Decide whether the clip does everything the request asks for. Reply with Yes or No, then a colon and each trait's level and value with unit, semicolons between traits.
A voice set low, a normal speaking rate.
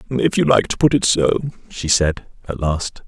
No: low, 110 Hz; fast, 215 wpm